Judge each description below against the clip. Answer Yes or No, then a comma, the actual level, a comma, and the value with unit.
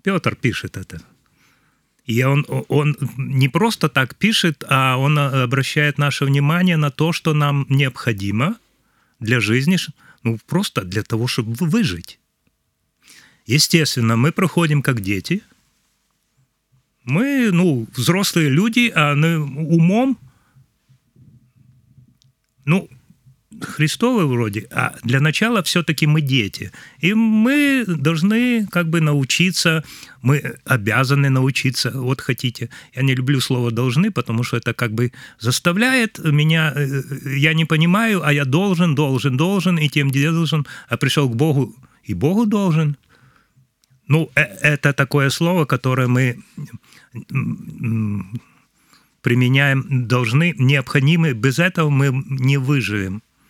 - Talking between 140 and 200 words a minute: No, average, 120 wpm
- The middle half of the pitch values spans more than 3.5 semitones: Yes, average, 4.2 semitones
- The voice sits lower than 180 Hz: Yes, medium, 140 Hz